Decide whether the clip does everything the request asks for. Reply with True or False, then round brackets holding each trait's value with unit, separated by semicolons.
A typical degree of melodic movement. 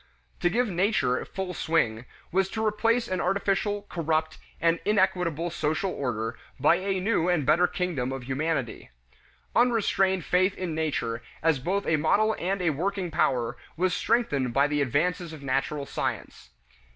True (4.9 semitones)